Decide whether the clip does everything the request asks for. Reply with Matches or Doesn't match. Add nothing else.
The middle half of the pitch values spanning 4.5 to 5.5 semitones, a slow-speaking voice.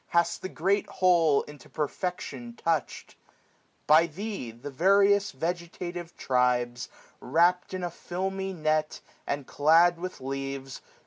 Matches